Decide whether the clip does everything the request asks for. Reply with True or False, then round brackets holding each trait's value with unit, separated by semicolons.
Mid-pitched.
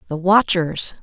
True (175 Hz)